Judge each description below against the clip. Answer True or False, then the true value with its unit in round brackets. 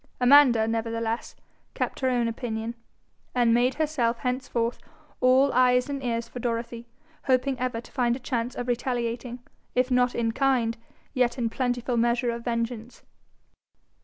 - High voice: True (245 Hz)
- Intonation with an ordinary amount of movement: False (1.5 semitones)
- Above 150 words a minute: False (145 wpm)